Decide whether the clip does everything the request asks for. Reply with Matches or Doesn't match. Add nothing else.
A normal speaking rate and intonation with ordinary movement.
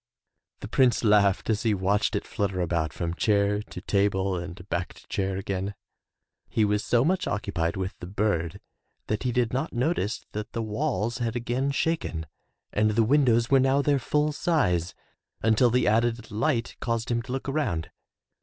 Matches